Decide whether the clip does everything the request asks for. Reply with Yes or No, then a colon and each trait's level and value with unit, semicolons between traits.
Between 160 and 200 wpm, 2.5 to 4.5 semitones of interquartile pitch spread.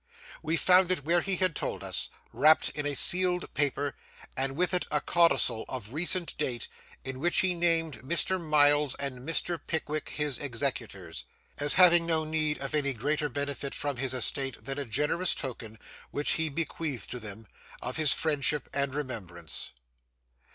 Yes: average, 165 wpm; average, 3.8 semitones